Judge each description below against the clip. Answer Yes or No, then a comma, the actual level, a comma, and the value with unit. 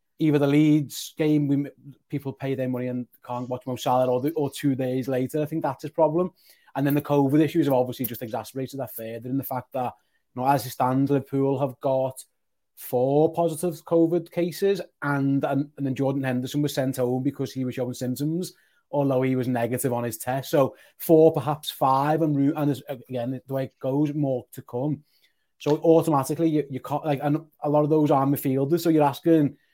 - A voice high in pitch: No, medium, 140 Hz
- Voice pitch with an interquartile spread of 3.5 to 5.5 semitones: No, average, 2.8 semitones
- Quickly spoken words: Yes, fast, 210 wpm